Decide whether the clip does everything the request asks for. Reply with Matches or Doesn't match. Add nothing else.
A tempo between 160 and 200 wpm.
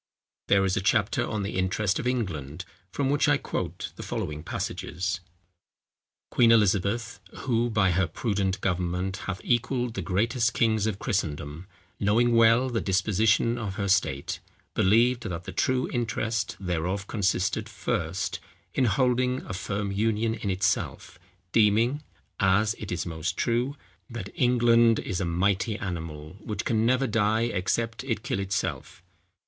Doesn't match